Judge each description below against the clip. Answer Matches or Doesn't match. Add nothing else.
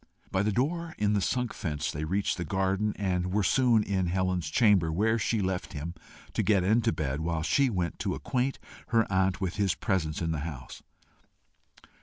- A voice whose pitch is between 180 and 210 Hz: Doesn't match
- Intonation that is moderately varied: Matches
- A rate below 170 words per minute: Doesn't match